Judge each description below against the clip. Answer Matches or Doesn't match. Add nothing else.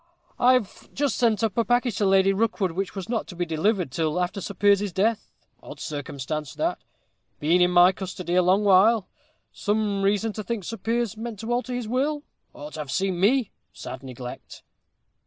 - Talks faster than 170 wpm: Matches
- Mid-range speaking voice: Doesn't match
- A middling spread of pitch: Matches